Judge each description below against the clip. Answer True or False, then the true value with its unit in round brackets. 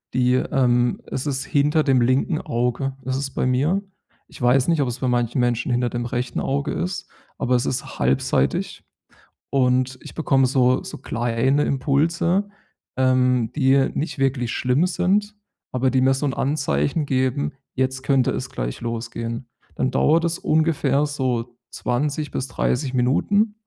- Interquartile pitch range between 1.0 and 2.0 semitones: False (2.8 semitones)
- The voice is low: True (130 Hz)